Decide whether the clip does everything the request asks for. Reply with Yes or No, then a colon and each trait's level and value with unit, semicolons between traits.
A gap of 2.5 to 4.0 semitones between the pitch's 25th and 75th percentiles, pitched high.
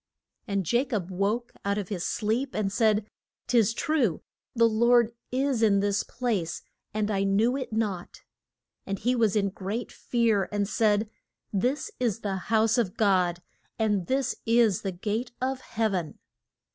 Yes: average, 3.1 semitones; high, 215 Hz